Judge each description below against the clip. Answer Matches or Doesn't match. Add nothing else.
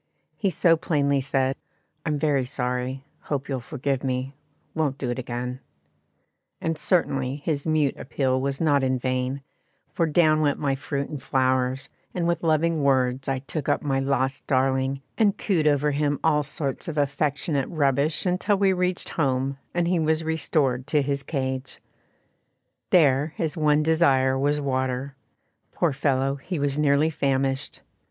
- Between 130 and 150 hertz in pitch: Matches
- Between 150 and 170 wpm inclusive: Matches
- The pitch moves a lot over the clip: Doesn't match